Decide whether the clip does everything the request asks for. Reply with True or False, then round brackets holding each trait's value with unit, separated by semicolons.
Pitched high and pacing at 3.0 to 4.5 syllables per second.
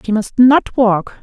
True (230 Hz; 4.0 syllables/s)